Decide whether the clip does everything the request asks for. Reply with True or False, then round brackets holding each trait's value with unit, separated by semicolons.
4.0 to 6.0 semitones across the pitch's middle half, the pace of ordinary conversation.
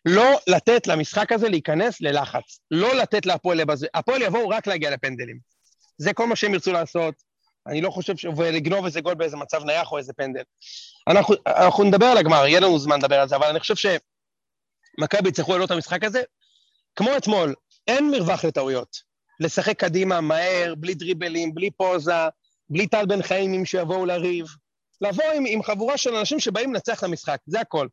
False (4.8 semitones; 185 wpm)